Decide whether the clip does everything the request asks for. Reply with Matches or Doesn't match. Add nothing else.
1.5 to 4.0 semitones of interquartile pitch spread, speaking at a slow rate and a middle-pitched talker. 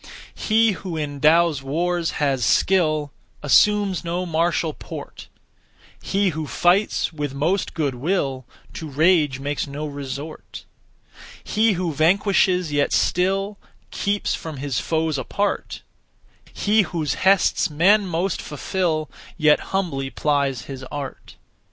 Doesn't match